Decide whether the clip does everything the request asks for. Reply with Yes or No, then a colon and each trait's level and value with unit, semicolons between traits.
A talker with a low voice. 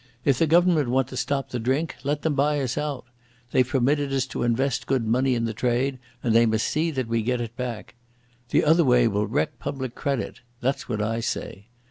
Yes: low, 130 Hz